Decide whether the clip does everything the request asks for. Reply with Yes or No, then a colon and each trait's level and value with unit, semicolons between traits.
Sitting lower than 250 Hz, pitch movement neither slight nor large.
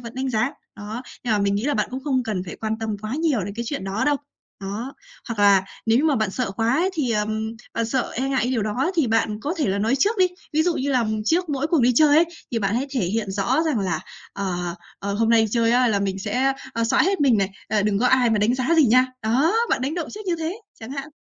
Yes: high, 235 Hz; average, 5.0 semitones